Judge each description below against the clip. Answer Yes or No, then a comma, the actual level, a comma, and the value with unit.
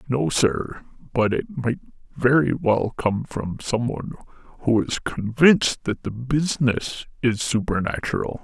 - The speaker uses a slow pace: Yes, slow, 130 wpm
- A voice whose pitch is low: Yes, low, 125 Hz